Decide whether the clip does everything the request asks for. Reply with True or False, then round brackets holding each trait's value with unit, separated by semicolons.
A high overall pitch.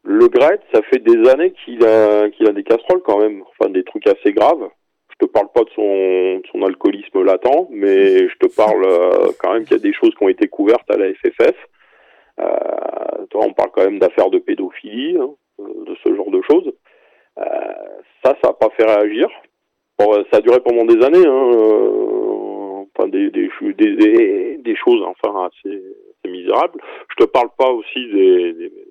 True (360 Hz)